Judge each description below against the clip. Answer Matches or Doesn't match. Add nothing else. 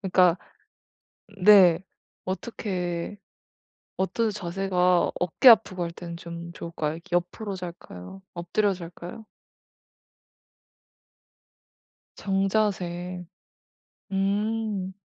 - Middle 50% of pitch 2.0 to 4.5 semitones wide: Matches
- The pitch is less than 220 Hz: Matches